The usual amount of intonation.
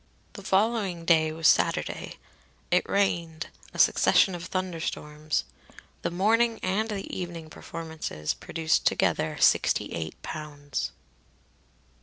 Yes: average, 3.5 semitones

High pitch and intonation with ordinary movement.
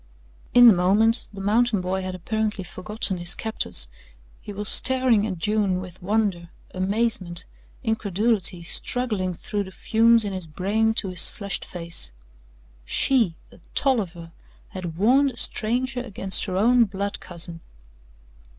Yes: high, 200 Hz; average, 3.5 semitones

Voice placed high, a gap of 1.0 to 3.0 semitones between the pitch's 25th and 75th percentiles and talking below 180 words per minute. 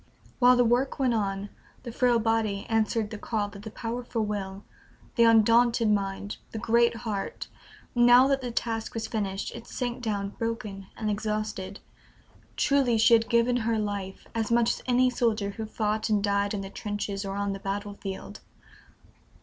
Yes: high, 220 Hz; average, 2.7 semitones; average, 170 wpm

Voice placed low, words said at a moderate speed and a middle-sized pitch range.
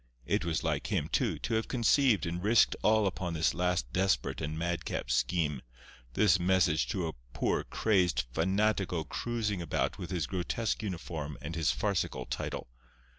Yes: very low, 90 Hz; average, 155 wpm; average, 4.2 semitones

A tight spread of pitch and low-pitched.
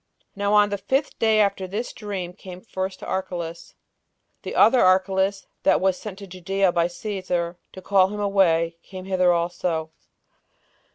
No: narrow, 2.2 semitones; high, 190 Hz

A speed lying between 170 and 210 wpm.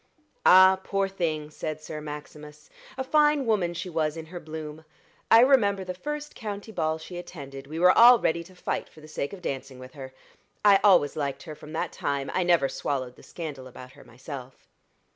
Yes: average, 200 wpm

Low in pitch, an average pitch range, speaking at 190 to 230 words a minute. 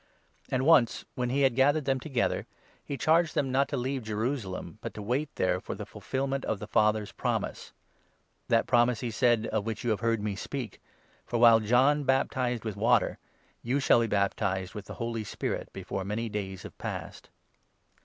Yes: low, 120 Hz; average, 3.8 semitones; average, 195 wpm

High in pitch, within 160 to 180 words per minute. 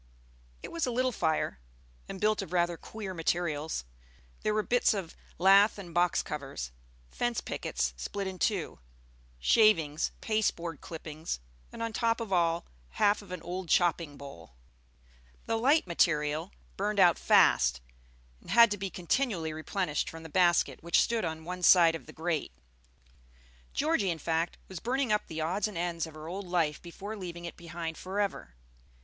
No: medium, 175 Hz; average, 165 wpm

